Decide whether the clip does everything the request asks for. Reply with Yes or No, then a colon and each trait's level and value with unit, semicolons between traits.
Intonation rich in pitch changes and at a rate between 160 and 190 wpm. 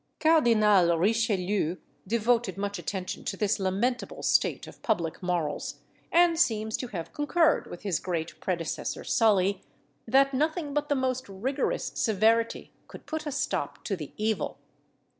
No: wide, 5.7 semitones; average, 140 wpm